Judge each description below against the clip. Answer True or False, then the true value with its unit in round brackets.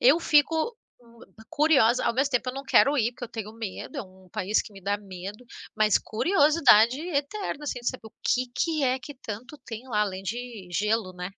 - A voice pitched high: True (240 Hz)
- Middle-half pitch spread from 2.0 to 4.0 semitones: False (5.1 semitones)